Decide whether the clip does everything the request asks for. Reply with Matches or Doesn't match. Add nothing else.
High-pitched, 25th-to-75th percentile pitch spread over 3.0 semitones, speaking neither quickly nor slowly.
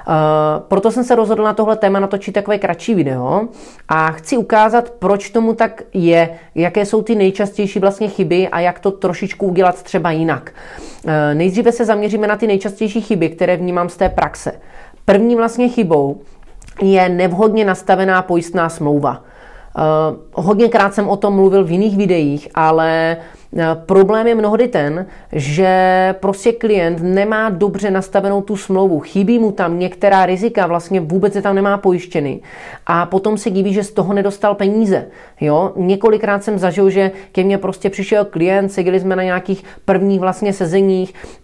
Doesn't match